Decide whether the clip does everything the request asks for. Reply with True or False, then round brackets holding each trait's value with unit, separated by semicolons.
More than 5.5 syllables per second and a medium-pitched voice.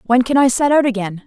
False (6.3 syllables/s; 245 Hz)